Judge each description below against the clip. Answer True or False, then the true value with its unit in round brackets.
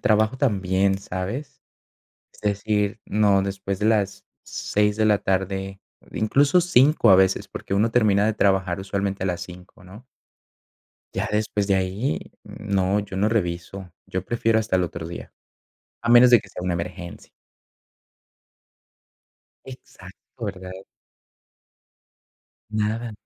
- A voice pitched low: True (100 Hz)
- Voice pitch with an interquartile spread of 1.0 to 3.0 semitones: True (2.5 semitones)